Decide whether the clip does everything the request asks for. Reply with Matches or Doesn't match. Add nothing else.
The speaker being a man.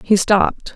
Doesn't match